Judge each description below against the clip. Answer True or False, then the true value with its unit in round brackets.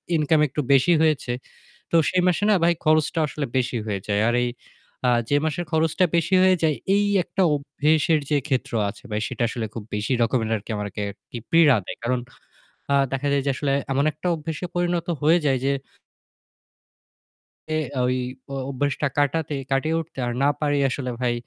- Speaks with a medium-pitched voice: True (145 Hz)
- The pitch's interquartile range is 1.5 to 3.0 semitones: False (3.9 semitones)